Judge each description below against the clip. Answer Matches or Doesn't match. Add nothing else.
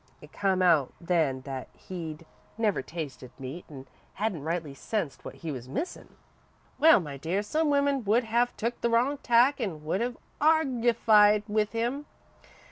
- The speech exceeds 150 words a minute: Matches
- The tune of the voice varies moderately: Doesn't match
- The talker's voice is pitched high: Matches